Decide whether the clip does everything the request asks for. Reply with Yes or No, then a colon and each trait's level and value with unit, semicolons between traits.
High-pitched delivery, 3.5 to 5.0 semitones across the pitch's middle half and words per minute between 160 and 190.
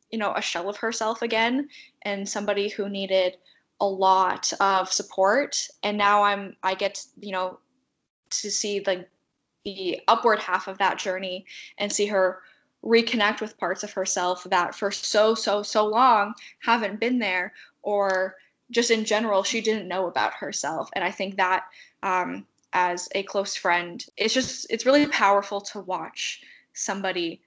No: high, 200 Hz; narrow, 2.5 semitones; average, 165 wpm